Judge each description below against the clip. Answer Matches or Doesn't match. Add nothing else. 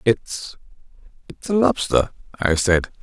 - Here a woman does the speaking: Doesn't match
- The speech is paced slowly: Matches